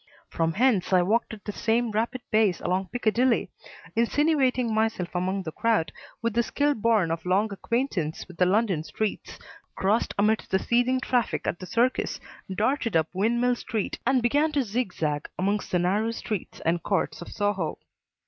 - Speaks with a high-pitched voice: Yes, high, 215 Hz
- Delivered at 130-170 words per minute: Yes, average, 165 wpm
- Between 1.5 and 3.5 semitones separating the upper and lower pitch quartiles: No, average, 4.4 semitones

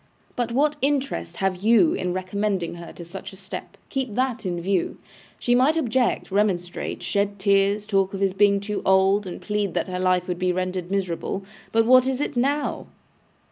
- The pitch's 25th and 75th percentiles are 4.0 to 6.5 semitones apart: Yes, average, 4.4 semitones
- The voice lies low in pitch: No, high, 200 Hz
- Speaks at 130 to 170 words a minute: No, average, 185 wpm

